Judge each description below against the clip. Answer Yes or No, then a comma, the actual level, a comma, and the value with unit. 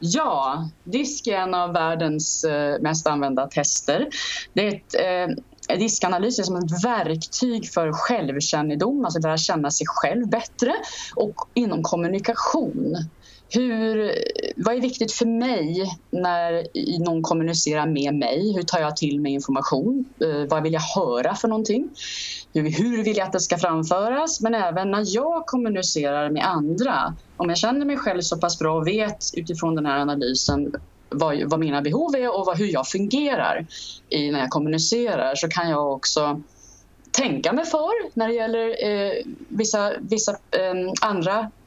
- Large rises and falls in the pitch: Yes, wide, 6.6 semitones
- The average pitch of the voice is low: No, medium, 185 Hz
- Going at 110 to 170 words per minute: Yes, average, 155 wpm